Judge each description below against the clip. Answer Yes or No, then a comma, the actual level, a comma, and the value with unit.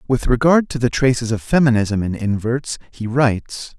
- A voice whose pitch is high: No, low, 120 Hz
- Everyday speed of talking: Yes, average, 175 wpm